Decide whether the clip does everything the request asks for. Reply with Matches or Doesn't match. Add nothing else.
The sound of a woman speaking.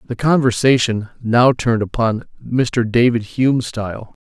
Doesn't match